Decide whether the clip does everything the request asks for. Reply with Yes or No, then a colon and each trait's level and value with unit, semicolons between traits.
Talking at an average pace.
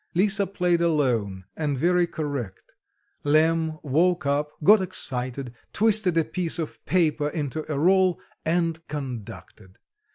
No: slow, 125 wpm